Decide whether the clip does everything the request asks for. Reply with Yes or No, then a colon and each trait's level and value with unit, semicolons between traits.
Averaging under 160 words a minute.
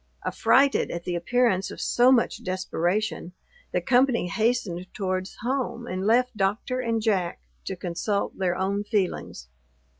Yes: average, 140 wpm